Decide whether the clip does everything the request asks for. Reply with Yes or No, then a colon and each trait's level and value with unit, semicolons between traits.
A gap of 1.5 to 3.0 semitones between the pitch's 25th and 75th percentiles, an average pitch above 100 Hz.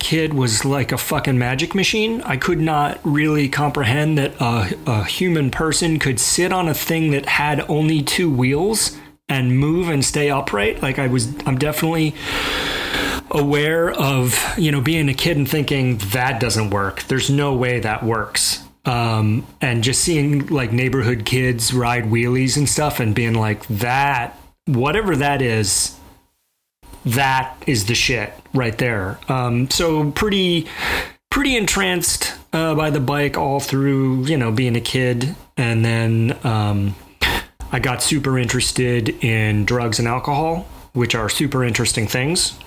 No: average, 4.0 semitones; low, 135 Hz